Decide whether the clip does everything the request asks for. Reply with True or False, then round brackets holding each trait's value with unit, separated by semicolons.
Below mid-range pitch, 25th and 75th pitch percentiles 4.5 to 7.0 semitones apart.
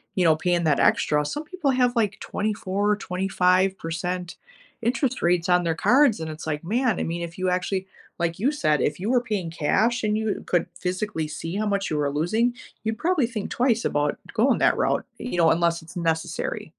False (185 Hz; 5.1 semitones)